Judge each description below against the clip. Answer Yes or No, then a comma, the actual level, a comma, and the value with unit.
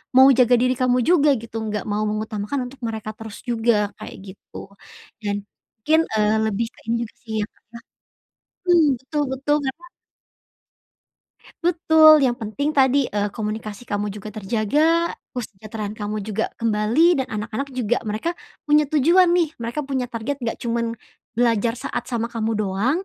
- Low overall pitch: No, high, 235 Hz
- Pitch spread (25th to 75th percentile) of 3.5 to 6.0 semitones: Yes, average, 4.3 semitones